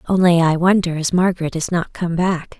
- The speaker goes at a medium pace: No, fast, 210 wpm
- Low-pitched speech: No, medium, 175 Hz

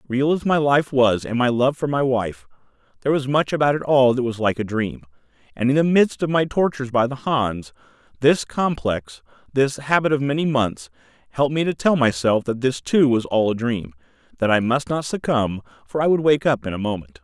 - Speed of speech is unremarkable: No, fast, 215 wpm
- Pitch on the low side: Yes, low, 130 Hz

